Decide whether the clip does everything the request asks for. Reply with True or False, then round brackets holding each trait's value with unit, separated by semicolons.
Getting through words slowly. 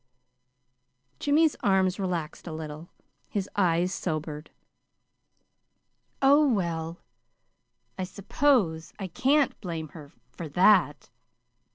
True (90 wpm)